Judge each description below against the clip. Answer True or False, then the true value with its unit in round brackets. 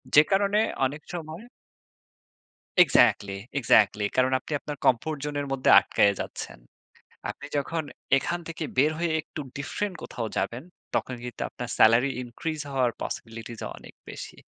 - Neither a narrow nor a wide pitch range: True (4.7 semitones)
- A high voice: False (140 Hz)